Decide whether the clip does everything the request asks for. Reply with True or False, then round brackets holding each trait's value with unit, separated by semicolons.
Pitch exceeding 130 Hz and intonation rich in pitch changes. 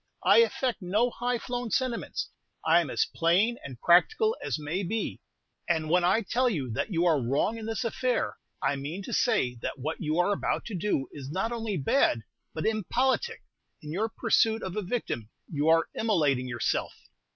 True (190 Hz; 6.9 semitones)